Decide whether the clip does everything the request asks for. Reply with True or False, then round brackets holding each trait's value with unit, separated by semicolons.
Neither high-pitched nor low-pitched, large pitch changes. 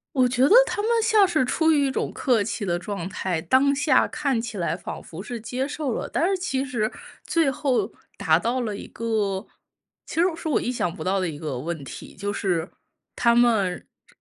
False (230 Hz; 6.4 semitones)